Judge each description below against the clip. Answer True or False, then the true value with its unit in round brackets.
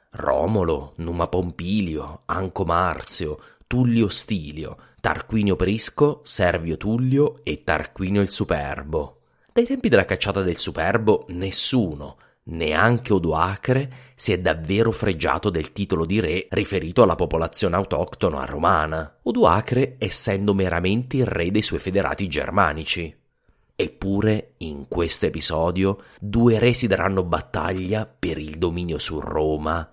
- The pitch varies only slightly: False (4.5 semitones)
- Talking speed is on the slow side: True (120 wpm)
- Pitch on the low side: True (95 Hz)